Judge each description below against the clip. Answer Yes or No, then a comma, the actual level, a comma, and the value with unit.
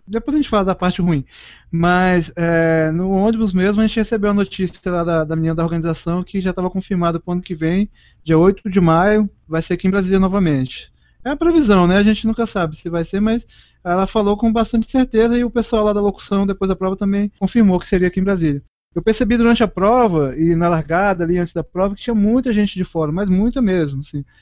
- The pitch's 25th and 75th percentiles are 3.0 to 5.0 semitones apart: Yes, average, 3.9 semitones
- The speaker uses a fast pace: Yes, fast, 240 wpm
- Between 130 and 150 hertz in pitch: No, high, 190 Hz